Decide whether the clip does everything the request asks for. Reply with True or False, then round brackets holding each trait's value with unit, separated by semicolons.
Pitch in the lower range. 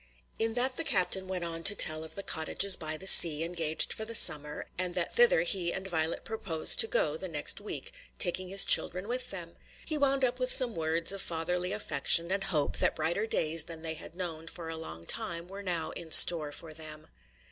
False (175 Hz)